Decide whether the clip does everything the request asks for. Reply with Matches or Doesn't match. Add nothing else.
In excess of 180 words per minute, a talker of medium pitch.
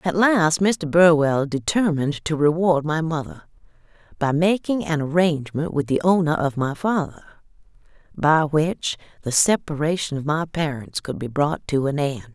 Doesn't match